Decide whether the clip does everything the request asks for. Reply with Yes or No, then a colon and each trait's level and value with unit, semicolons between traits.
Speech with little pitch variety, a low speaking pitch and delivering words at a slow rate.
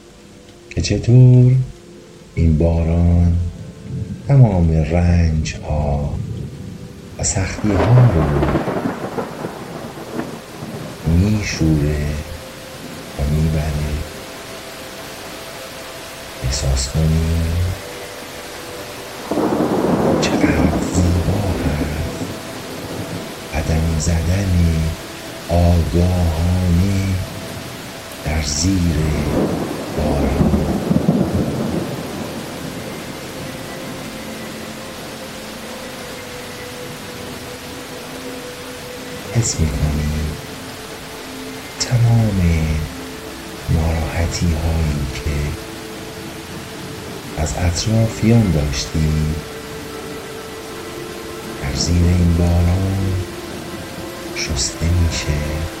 No: average, 3.2 semitones; very low, 85 Hz; slow, 40 wpm